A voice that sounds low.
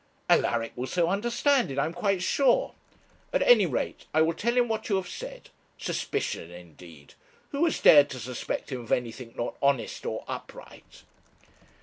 No: medium, 160 Hz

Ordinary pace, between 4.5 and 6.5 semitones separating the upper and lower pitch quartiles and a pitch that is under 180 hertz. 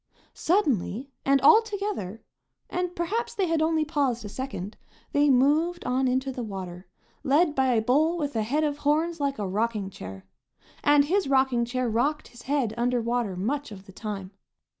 No: average, 180 wpm; wide, 5.4 semitones; very high, 265 Hz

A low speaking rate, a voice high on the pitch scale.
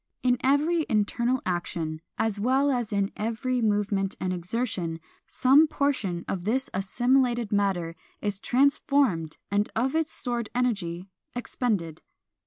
Yes: slow, 125 wpm; high, 220 Hz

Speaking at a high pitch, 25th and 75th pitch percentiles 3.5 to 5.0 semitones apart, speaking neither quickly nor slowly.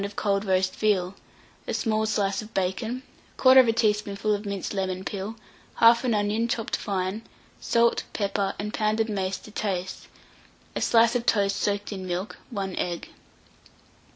No: high, 205 Hz; narrow, 2.5 semitones; average, 150 wpm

